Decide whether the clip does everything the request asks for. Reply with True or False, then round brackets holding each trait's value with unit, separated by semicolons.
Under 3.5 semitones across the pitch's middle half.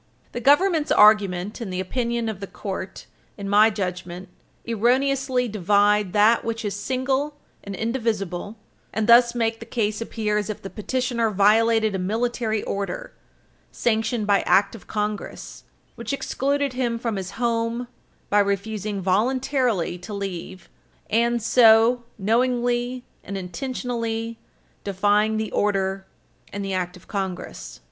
True (3.1 semitones)